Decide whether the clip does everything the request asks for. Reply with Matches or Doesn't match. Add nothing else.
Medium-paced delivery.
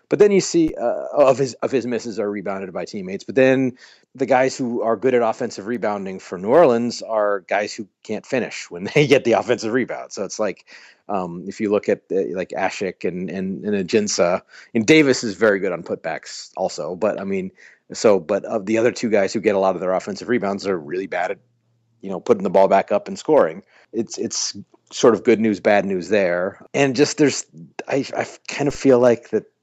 Doesn't match